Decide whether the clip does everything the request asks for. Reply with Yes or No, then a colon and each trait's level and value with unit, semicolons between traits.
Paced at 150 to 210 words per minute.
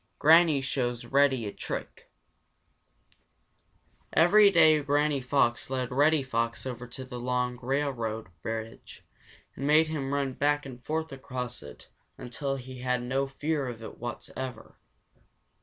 No: slow, 135 wpm